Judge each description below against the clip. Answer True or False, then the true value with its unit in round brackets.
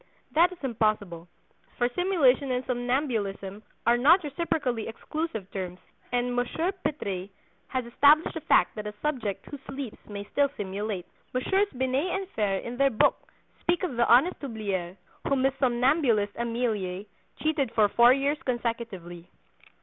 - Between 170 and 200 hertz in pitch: False (245 Hz)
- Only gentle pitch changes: False (5.3 semitones)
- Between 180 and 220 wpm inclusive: False (145 wpm)